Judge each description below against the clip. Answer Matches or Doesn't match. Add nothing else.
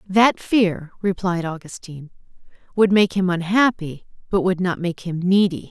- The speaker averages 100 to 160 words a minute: Matches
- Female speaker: Matches